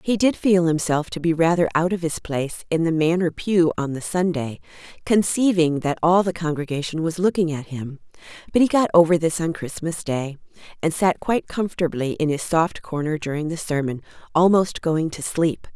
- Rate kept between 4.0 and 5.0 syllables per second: No, 5.3 syllables/s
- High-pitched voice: No, medium, 165 Hz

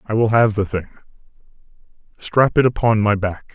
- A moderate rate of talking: Yes, average, 170 wpm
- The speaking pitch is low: Yes, low, 105 Hz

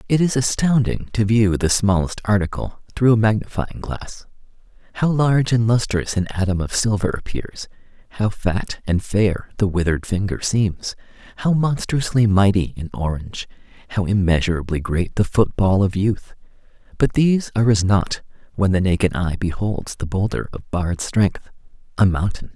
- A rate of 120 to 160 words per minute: Yes, average, 155 wpm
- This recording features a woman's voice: No, male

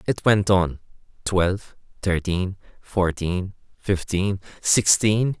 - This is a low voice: Yes, very low, 95 Hz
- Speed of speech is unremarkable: No, slow, 80 wpm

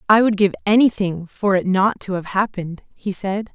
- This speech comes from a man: No, female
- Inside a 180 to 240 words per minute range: Yes, fast, 205 wpm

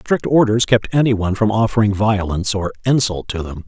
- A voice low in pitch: Yes, low, 105 Hz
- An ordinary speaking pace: Yes, average, 180 wpm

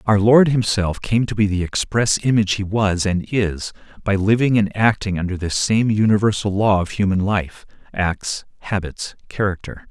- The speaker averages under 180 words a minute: Yes, average, 165 wpm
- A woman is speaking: No, male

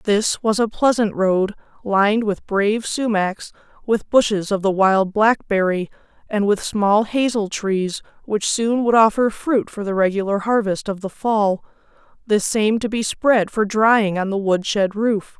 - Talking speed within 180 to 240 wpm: No, average, 170 wpm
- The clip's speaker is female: Yes, female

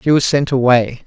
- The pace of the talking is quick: Yes, fast, 225 wpm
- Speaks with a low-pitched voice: Yes, low, 130 Hz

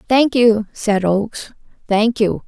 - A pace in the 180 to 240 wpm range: No, average, 145 wpm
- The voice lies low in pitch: No, high, 220 Hz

